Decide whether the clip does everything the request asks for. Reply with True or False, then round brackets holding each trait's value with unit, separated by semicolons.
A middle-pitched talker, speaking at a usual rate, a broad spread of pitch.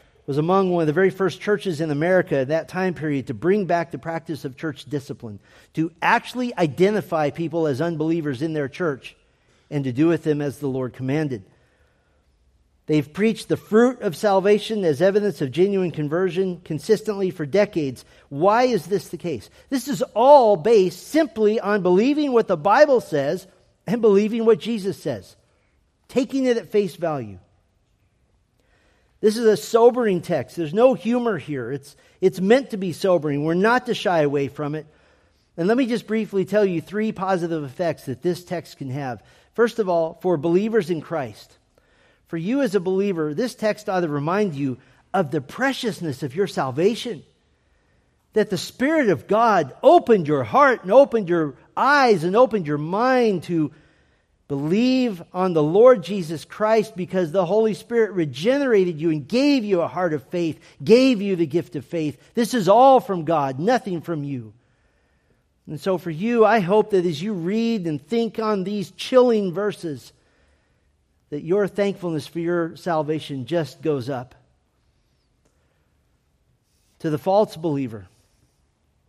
True (175 Hz; 165 wpm; 6.2 semitones)